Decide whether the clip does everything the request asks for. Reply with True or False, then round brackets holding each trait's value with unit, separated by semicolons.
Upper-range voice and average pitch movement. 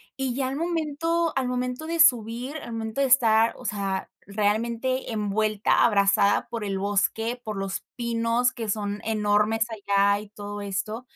True (225 Hz; 3.5 semitones)